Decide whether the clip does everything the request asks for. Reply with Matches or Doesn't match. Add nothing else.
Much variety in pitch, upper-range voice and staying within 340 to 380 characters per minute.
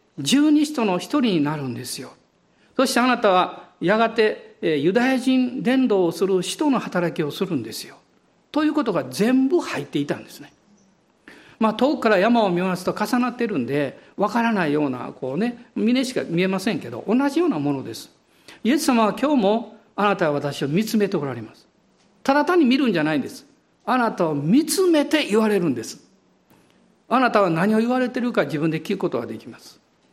Matches